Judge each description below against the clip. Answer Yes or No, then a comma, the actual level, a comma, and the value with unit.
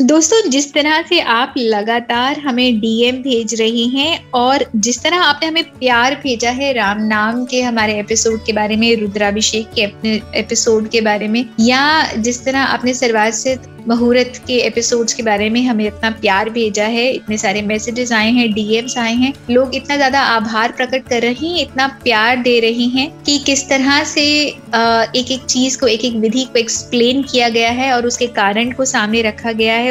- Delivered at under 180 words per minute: No, fast, 190 wpm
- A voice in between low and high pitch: No, high, 240 Hz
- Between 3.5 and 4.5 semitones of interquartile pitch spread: No, average, 2.8 semitones